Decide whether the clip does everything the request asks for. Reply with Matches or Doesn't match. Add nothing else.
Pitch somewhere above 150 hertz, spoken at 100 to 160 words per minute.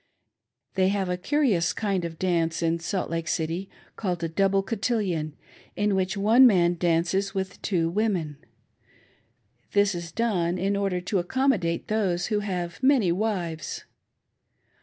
Matches